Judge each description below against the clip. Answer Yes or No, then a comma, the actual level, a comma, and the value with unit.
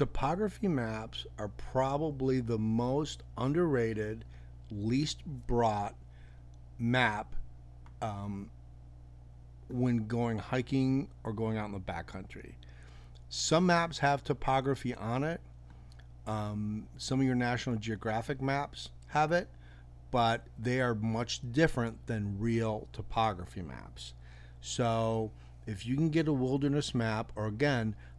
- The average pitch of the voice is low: Yes, low, 110 Hz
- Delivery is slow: Yes, slow, 115 wpm